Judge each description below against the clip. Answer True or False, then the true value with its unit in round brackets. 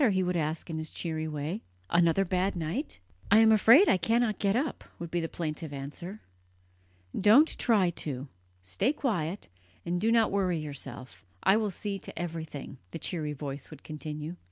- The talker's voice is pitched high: False (175 Hz)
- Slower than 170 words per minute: False (175 wpm)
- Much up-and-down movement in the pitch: False (5.0 semitones)